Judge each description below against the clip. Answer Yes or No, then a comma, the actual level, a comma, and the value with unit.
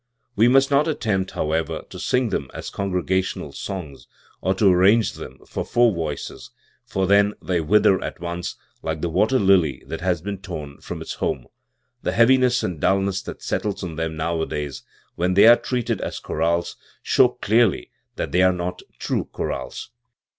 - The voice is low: Yes, very low, 95 Hz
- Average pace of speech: Yes, average, 175 wpm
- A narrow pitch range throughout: No, average, 4.3 semitones